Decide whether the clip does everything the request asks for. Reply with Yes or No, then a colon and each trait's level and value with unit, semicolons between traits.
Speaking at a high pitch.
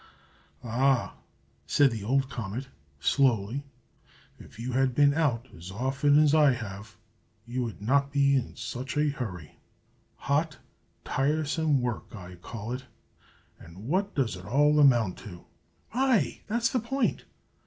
No: low, 130 Hz